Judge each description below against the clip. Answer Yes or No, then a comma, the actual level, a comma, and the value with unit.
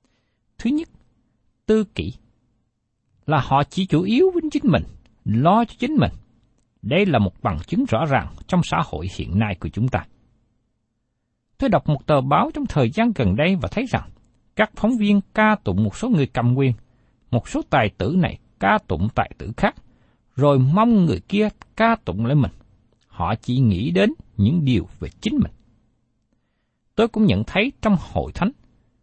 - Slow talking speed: No, average, 180 wpm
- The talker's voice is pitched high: No, low, 130 Hz